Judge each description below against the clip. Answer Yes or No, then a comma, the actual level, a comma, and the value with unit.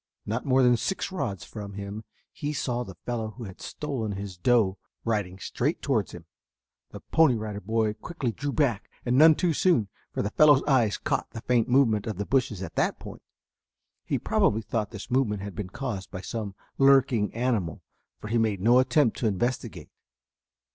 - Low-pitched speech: Yes, low, 115 Hz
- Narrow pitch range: No, average, 4.2 semitones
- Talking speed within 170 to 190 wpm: Yes, average, 185 wpm